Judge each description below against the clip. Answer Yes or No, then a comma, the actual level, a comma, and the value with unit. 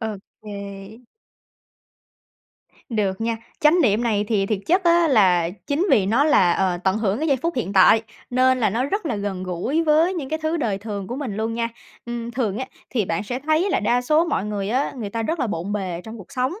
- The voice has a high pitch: Yes, high, 230 Hz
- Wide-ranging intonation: Yes, wide, 5.7 semitones